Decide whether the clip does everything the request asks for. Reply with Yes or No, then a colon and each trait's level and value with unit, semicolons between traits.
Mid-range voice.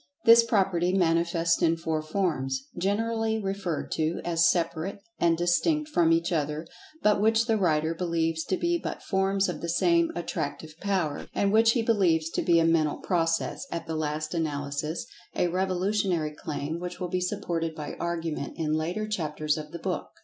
Yes: medium, 170 Hz